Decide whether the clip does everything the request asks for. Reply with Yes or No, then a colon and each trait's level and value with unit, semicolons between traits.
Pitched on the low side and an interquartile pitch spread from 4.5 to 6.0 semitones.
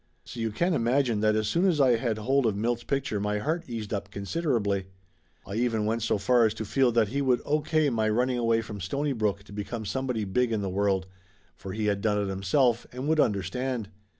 No: low, 115 Hz; average, 4.0 semitones